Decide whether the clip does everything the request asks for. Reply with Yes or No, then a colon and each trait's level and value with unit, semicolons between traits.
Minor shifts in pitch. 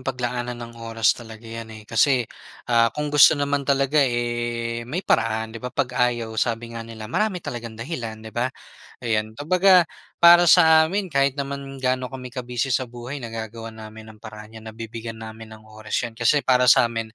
No: average, 3.4 semitones